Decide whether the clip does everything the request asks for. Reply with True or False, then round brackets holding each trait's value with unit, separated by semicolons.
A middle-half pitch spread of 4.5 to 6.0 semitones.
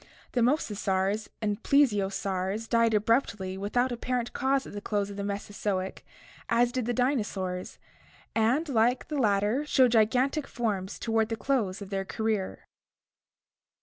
False (3.6 semitones)